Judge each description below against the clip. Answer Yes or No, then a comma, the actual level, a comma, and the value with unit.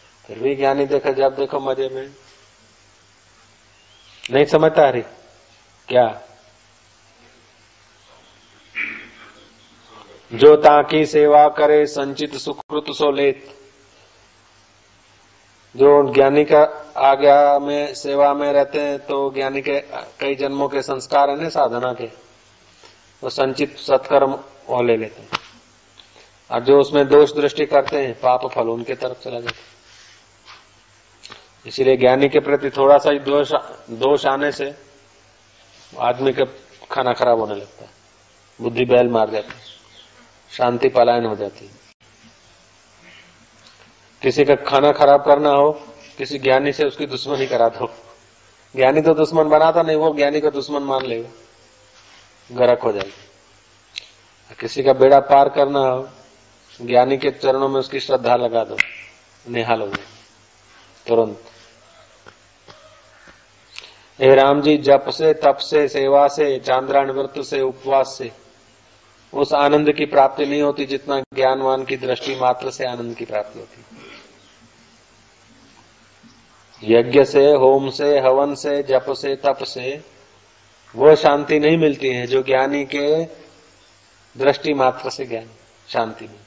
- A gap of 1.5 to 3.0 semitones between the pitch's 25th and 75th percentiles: No, average, 3.8 semitones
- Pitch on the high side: No, low, 135 Hz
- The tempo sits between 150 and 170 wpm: No, average, 125 wpm